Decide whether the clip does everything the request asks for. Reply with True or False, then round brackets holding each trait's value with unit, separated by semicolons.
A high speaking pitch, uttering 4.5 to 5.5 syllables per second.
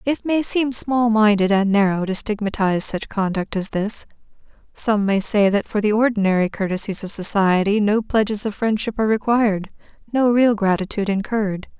True (210 Hz; 5.3 syllables/s)